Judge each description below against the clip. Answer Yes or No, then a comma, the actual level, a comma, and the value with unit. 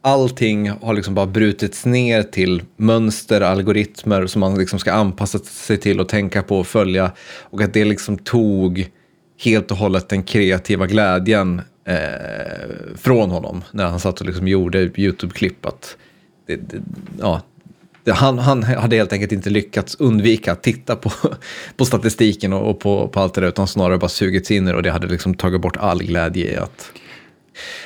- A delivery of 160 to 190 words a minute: Yes, average, 170 wpm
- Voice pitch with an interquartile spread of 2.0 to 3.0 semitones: Yes, narrow, 2.4 semitones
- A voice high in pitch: No, low, 100 Hz